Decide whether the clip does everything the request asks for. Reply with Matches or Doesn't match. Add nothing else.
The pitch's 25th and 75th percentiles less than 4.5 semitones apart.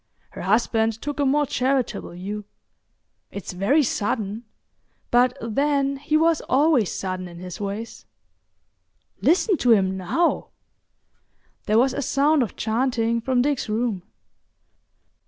Doesn't match